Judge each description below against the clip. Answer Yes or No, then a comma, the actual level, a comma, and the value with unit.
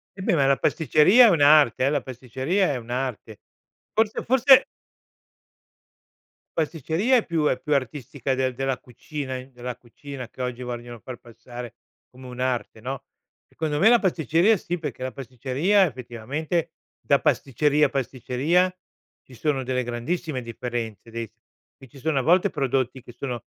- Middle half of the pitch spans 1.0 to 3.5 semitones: No, average, 4.3 semitones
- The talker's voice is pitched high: No, low, 135 Hz